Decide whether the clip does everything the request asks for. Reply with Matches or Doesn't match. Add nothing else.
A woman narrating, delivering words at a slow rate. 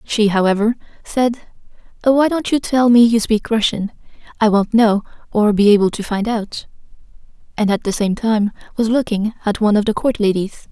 Doesn't match